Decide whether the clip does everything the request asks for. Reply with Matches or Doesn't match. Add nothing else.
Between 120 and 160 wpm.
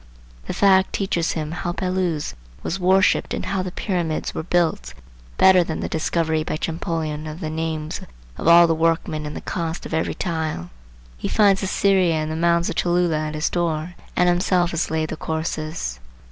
Doesn't match